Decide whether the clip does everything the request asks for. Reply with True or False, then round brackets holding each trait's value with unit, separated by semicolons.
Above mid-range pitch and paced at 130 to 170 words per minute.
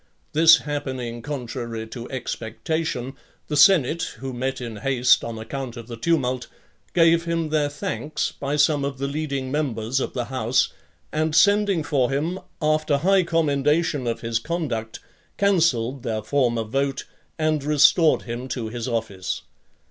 False (140 Hz; 150 wpm)